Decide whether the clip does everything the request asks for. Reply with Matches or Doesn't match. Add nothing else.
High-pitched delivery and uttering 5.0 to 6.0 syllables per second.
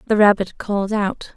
Matches